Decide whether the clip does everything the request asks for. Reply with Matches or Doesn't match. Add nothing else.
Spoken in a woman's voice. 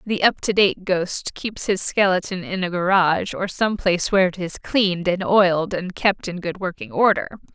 Matches